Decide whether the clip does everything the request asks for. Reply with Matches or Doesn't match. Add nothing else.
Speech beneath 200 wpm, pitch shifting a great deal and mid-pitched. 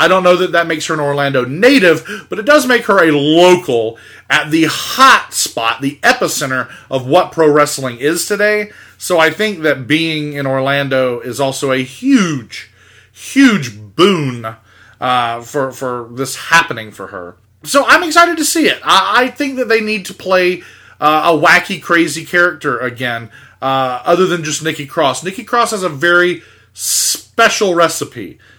Matches